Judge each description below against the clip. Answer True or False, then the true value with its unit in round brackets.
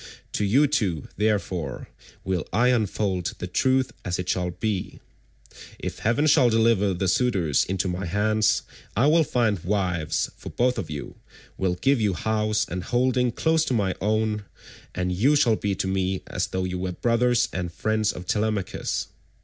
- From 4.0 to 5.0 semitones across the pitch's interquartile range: True (4.3 semitones)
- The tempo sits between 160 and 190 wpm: True (170 wpm)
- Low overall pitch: True (105 Hz)